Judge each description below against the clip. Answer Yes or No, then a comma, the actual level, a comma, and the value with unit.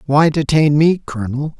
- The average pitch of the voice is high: No, medium, 150 Hz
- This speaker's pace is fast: No, average, 150 wpm